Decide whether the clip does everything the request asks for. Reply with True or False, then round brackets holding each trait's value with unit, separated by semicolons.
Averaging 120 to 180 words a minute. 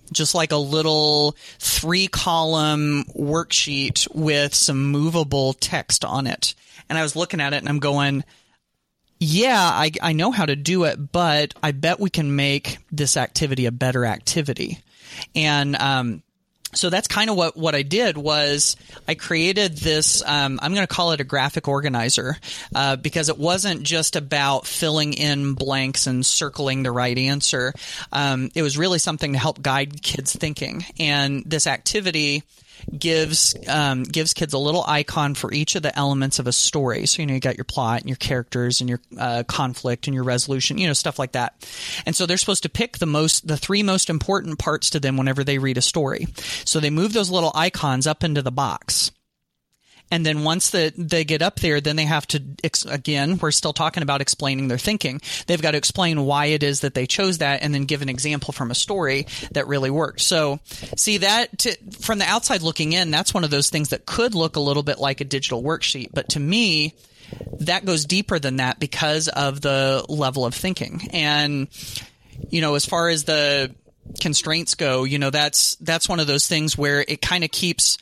False (200 wpm)